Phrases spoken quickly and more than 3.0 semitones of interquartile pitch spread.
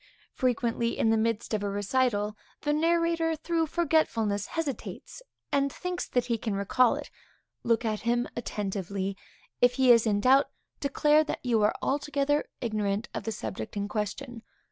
No: average, 160 wpm; wide, 5.4 semitones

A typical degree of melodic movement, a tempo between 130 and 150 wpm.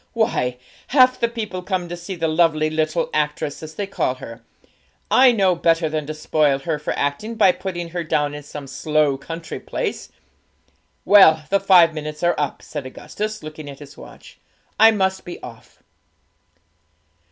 No: average, 4.1 semitones; average, 170 wpm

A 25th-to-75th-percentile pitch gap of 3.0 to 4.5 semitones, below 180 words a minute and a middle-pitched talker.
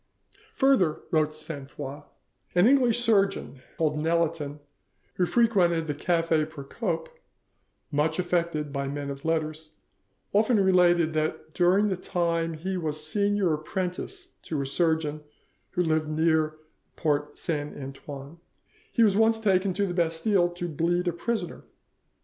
Yes: average, 3.5 semitones; average, 140 wpm; medium, 165 Hz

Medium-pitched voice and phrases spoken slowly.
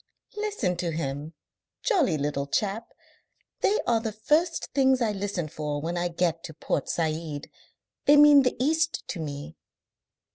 No: medium, 180 Hz; average, 150 wpm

